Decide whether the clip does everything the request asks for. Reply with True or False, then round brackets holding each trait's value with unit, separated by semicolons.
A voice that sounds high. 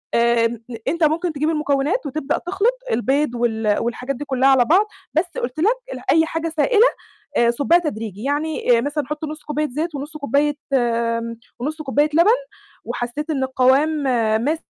True (295 Hz)